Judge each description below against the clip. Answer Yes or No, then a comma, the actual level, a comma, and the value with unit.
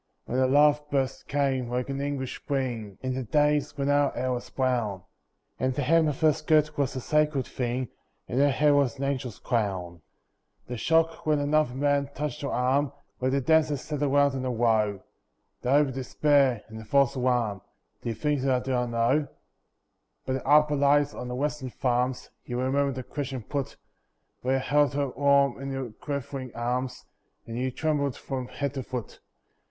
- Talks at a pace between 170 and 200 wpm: Yes, average, 190 wpm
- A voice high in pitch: No, low, 135 Hz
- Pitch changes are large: No, narrow, 2.4 semitones